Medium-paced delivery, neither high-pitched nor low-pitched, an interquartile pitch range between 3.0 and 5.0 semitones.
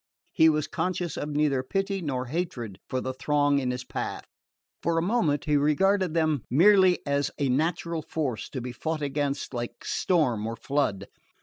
Yes: average, 175 wpm; medium, 145 Hz; average, 4.3 semitones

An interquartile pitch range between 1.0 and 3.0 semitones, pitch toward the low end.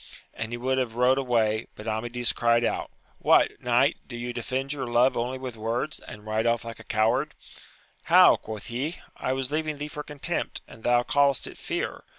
Yes: narrow, 2.4 semitones; low, 120 Hz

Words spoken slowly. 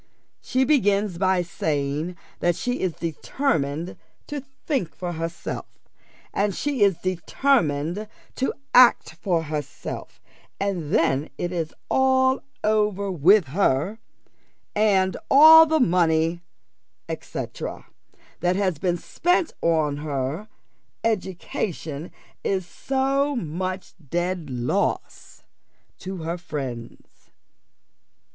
Yes: slow, 100 wpm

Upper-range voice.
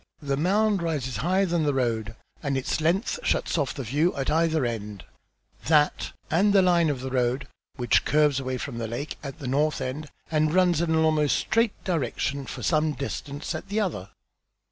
No: medium, 150 Hz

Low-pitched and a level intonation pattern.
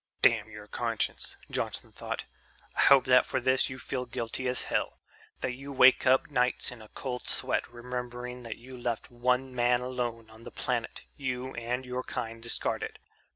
Yes: low, 125 Hz; narrow, 1.4 semitones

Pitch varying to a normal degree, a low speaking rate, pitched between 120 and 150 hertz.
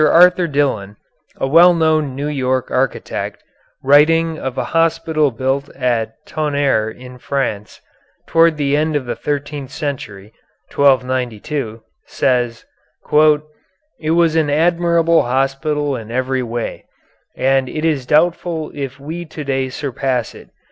Yes: average, 3.5 semitones; slow, 125 wpm; medium, 140 Hz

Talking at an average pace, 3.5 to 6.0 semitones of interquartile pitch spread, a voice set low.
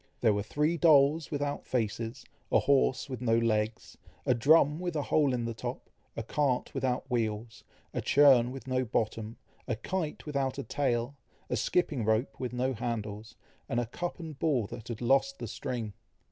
Yes: average, 180 wpm; average, 3.8 semitones; low, 125 Hz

